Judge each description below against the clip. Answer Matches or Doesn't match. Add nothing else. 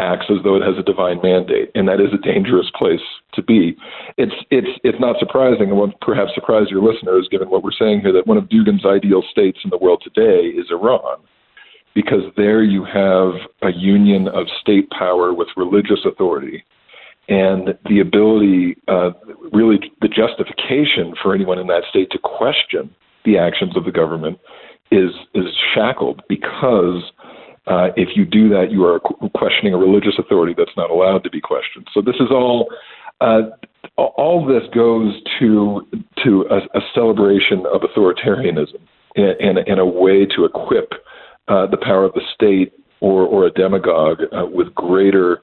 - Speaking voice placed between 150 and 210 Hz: Doesn't match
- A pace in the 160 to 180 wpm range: Matches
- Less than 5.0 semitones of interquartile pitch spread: Matches